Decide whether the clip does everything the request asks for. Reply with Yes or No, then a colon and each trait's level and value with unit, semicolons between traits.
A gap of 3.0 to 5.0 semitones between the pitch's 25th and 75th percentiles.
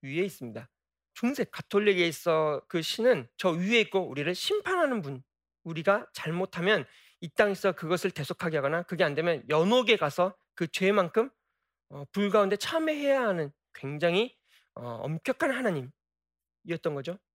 No: wide, 5.6 semitones